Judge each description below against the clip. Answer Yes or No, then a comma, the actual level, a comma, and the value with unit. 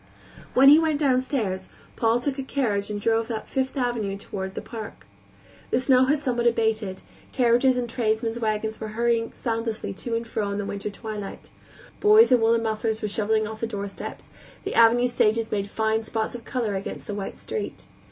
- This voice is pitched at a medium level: No, high, 225 Hz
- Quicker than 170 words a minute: Yes, average, 185 wpm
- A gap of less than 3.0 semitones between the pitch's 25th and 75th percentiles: Yes, narrow, 2.4 semitones